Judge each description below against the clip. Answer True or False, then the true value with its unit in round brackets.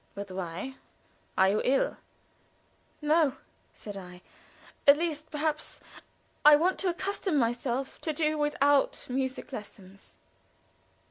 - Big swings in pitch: True (6.5 semitones)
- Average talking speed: False (115 wpm)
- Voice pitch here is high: True (275 Hz)